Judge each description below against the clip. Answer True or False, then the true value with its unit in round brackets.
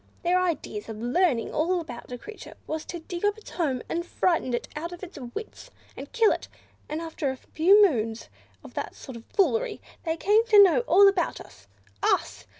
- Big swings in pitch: True (7.0 semitones)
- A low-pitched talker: False (340 Hz)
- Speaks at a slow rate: False (200 wpm)